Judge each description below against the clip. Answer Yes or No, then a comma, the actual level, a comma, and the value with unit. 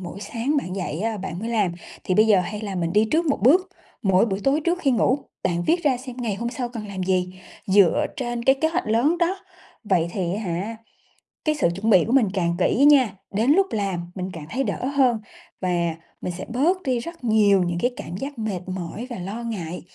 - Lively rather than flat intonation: Yes, wide, 5.8 semitones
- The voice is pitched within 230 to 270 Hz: No, high, 215 Hz